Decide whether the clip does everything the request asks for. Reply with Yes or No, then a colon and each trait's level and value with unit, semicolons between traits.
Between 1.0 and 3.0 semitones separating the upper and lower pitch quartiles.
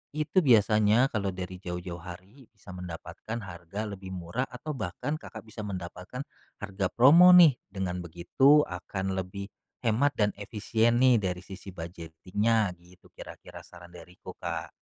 No: average, 4.3 semitones